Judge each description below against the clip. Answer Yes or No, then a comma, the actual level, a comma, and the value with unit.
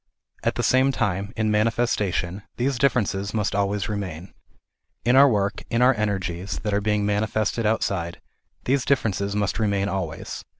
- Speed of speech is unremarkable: Yes, average, 155 wpm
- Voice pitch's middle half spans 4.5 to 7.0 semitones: No, average, 2.7 semitones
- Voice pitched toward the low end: Yes, low, 105 Hz